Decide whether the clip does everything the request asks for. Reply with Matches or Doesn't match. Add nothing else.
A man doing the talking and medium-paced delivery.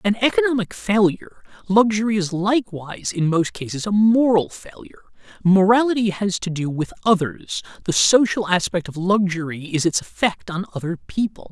Matches